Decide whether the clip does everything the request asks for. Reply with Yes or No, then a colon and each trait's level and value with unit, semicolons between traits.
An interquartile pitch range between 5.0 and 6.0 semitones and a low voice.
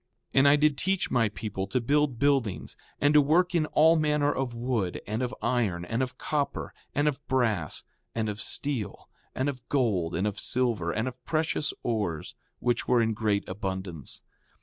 Yes: wide, 5.5 semitones; low, 125 Hz